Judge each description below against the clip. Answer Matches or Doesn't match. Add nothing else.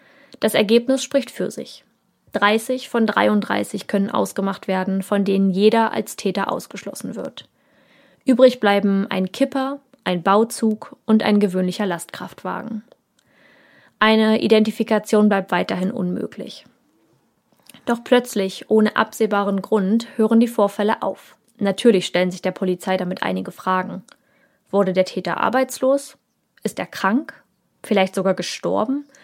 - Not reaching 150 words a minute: Matches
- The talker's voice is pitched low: Doesn't match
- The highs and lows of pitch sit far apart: Doesn't match